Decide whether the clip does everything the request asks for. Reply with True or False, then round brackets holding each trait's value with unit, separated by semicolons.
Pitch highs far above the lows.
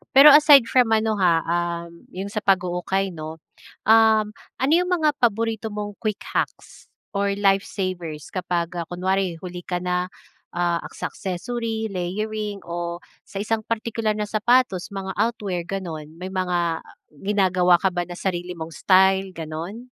False (3.6 semitones)